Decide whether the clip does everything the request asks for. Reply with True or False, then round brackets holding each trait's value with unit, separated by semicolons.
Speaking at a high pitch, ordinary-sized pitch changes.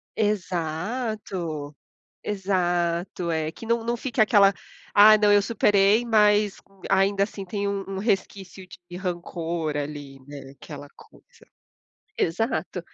True (195 Hz; 3.6 semitones)